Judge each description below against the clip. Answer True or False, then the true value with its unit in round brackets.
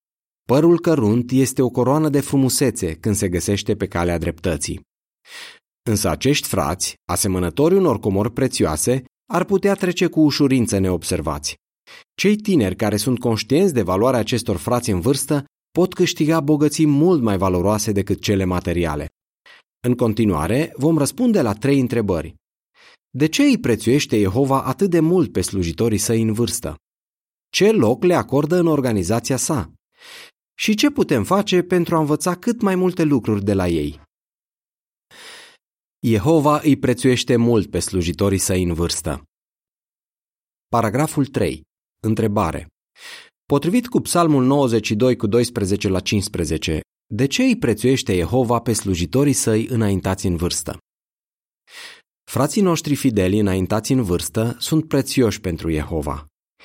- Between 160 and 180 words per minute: False (135 wpm)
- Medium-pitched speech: False (120 Hz)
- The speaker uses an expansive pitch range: True (7.7 semitones)